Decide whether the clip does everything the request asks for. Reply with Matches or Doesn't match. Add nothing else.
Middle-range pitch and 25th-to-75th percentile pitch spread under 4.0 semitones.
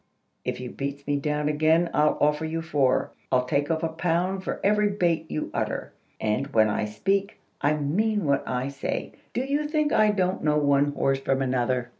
Doesn't match